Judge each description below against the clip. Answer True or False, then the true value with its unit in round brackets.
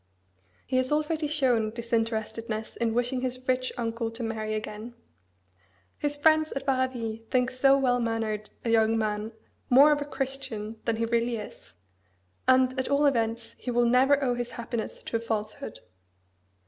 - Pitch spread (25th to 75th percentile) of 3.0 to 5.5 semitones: False (2.6 semitones)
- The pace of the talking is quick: False (160 wpm)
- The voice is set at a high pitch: True (240 Hz)